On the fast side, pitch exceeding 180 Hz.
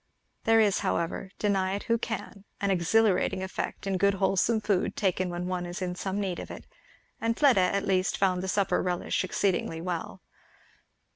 No: average, 180 wpm; high, 190 Hz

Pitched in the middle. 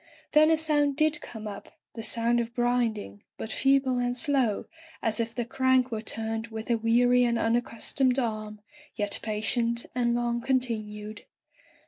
No: high, 235 Hz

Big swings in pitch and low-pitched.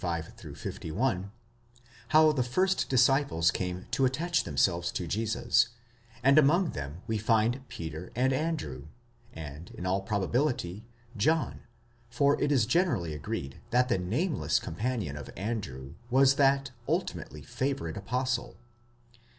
Yes: wide, 7.7 semitones; low, 115 Hz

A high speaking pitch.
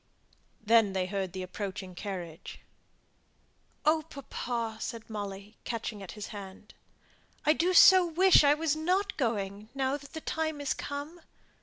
Yes: high, 230 Hz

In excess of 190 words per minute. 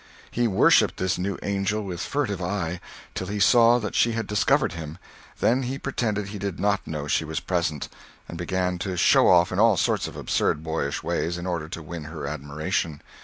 Yes: average, 200 wpm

